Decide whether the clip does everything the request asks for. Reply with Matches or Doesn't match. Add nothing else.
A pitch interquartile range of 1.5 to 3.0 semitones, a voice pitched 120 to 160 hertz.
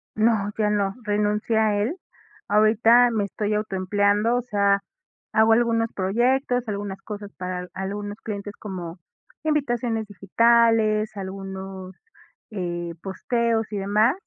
Doesn't match